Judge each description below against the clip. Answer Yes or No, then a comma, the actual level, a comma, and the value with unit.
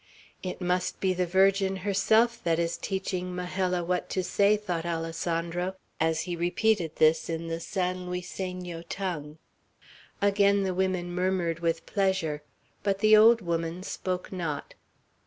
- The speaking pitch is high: No, medium, 180 Hz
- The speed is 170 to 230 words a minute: No, average, 140 wpm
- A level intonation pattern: Yes, narrow, 2.3 semitones